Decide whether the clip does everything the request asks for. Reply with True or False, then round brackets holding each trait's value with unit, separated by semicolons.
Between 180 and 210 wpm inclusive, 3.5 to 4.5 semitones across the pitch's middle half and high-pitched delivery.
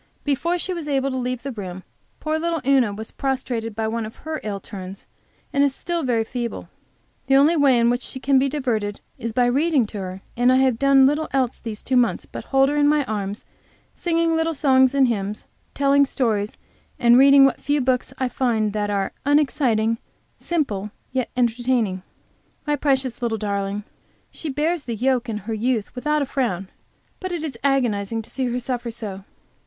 True (195 wpm; 4.0 semitones; 255 Hz)